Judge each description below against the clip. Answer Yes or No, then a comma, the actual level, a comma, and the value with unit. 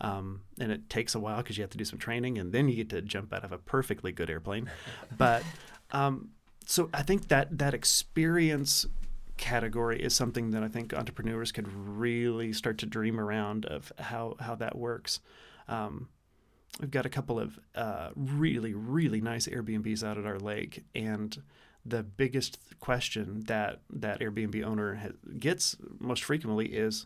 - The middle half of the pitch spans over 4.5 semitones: No, average, 2.9 semitones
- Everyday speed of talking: Yes, average, 175 wpm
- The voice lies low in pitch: Yes, low, 115 Hz